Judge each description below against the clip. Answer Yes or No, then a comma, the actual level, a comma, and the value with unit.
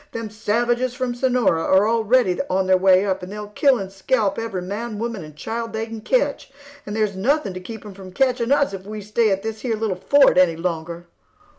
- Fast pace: Yes, fast, 220 wpm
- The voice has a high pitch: Yes, high, 215 Hz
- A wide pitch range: No, average, 3.8 semitones